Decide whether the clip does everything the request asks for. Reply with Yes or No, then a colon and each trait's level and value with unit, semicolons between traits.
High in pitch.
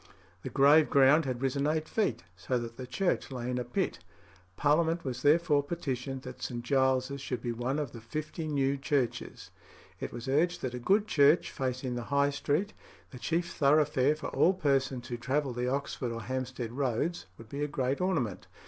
No: low, 135 Hz